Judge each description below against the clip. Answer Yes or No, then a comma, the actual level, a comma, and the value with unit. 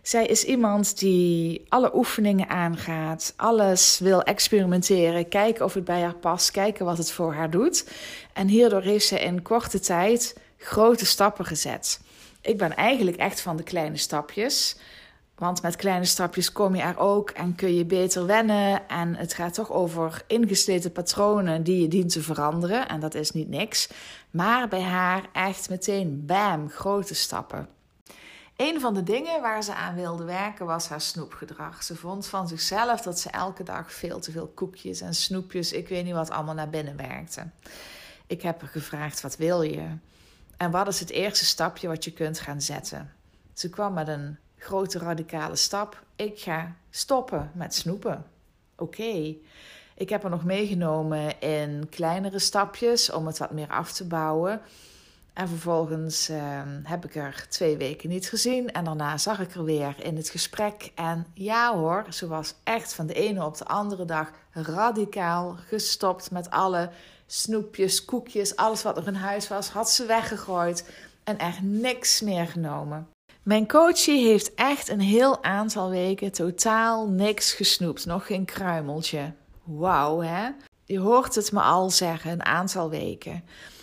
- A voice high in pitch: No, medium, 180 Hz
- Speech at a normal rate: Yes, average, 170 wpm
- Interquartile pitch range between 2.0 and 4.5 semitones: Yes, average, 3.8 semitones